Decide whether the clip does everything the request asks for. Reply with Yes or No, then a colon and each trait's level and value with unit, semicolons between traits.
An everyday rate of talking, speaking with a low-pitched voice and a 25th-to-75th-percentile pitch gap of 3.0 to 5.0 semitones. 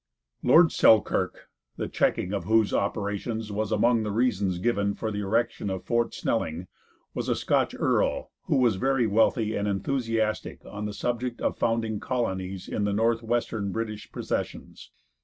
No: average, 155 wpm; low, 110 Hz; narrow, 2.5 semitones